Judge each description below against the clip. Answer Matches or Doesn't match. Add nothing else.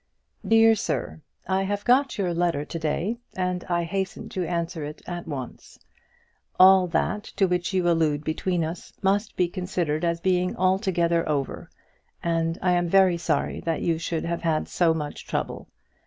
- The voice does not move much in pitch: Matches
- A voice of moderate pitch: Matches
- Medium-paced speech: Matches